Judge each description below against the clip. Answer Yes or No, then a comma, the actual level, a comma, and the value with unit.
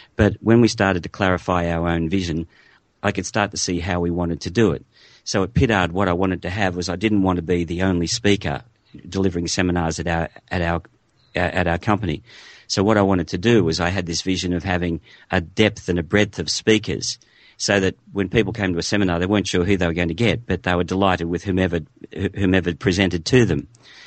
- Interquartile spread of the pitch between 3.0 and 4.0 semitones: No, narrow, 2.5 semitones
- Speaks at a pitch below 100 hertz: Yes, very low, 90 Hz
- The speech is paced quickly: Yes, fast, 230 wpm